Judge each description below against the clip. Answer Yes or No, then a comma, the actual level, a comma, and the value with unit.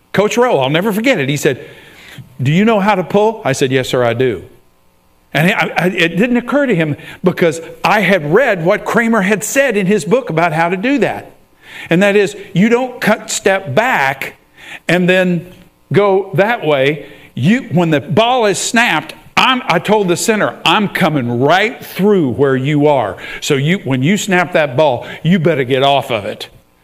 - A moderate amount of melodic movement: No, wide, 6.3 semitones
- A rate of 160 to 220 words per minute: Yes, average, 190 wpm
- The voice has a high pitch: No, medium, 180 Hz